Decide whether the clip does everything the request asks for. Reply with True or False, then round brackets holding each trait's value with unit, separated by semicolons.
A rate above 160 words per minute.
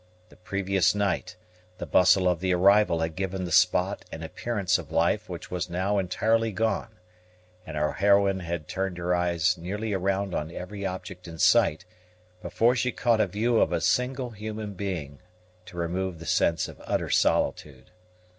True (170 wpm)